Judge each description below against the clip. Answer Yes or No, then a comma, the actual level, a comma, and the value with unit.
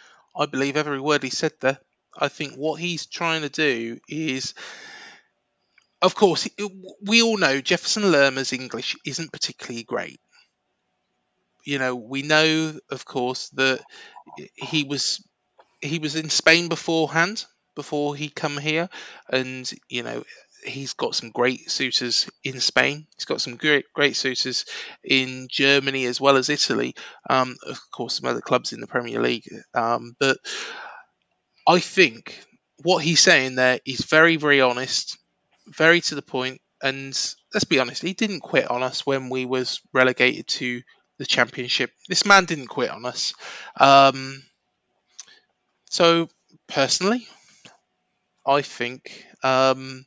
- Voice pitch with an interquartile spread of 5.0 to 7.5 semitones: No, average, 4.1 semitones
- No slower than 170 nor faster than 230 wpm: No, average, 145 wpm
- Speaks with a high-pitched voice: No, medium, 140 Hz